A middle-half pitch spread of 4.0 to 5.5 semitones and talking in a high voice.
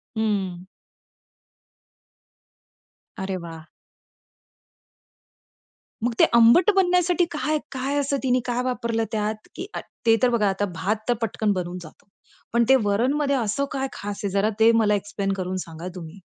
Yes: average, 5.0 semitones; high, 220 Hz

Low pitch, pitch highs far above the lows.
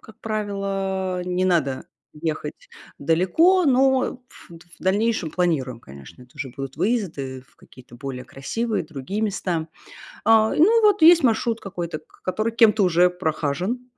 No: medium, 185 Hz; wide, 6.5 semitones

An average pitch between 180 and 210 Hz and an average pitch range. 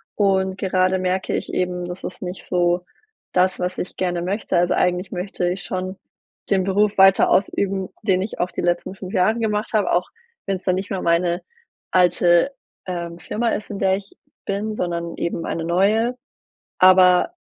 No: medium, 185 Hz; narrow, 1.7 semitones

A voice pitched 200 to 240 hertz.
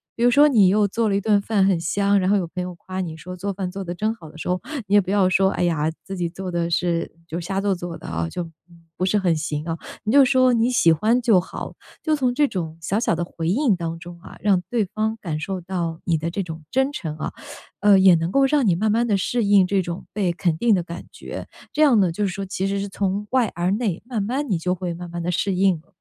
No: high, 190 Hz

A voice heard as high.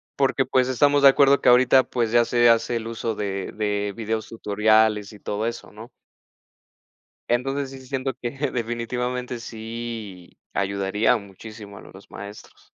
No: low, 115 Hz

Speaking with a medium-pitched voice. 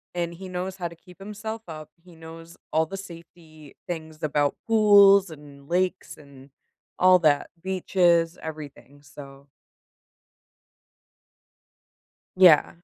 Yes: medium, 170 Hz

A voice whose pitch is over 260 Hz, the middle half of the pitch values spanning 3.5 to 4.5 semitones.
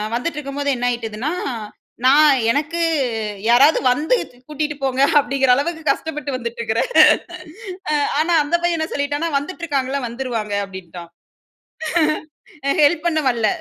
Yes: very high, 280 Hz; average, 4.1 semitones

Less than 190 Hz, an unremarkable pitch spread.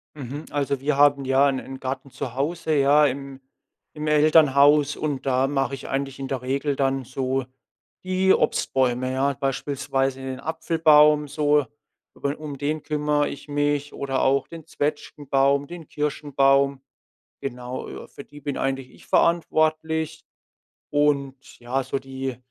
No: medium, 140 Hz; narrow, 1.8 semitones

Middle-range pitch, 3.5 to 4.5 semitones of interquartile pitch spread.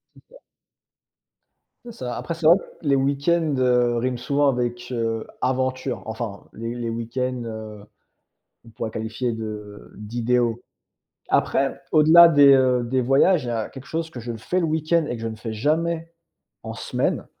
No: low, 125 Hz; average, 4.0 semitones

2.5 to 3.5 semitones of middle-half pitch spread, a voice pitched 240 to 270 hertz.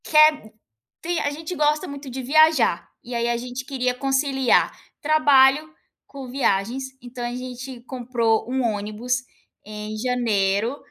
Yes: average, 3.1 semitones; very high, 255 Hz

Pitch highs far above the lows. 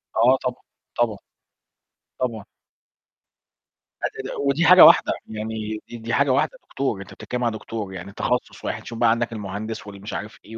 No: average, 2.7 semitones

